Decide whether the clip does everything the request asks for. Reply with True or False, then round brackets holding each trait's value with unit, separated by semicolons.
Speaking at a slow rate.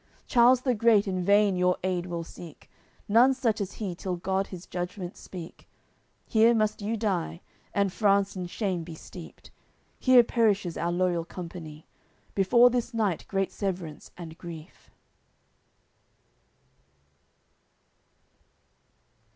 True (125 wpm)